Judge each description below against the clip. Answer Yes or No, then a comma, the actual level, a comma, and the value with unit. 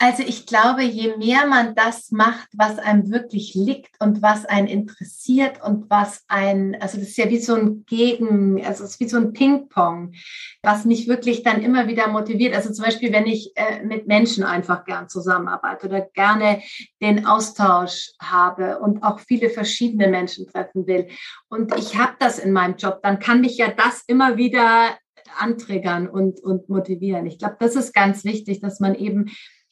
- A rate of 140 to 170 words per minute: No, average, 185 wpm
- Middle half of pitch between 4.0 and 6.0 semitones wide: No, average, 2.9 semitones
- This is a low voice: No, high, 210 Hz